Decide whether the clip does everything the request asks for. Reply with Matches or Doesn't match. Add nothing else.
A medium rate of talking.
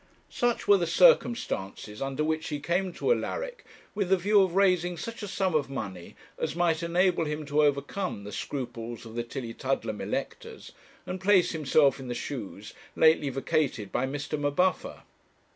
Matches